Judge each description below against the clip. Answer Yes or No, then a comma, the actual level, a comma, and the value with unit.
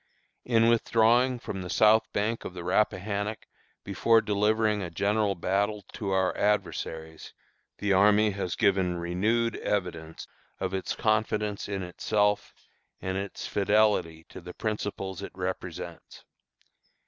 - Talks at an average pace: No, slow, 125 wpm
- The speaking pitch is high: No, low, 100 Hz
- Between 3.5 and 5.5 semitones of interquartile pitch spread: No, average, 2.7 semitones